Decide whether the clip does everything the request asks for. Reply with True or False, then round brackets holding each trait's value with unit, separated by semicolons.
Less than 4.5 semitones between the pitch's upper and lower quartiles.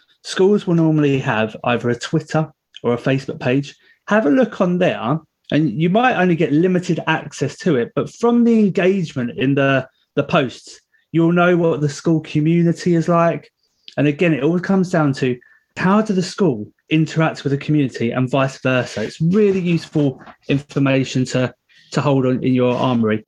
False (4.9 semitones)